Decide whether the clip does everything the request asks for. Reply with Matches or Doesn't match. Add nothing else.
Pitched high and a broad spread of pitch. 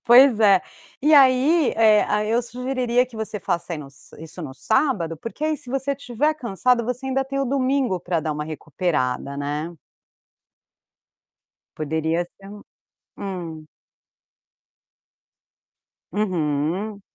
Matches